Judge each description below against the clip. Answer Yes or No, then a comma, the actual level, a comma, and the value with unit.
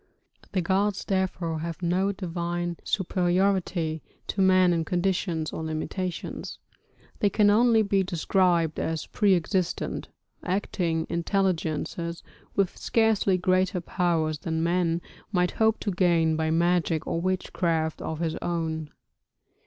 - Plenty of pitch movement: No, narrow, 2.5 semitones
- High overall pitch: No, medium, 175 Hz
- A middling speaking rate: No, slow, 120 wpm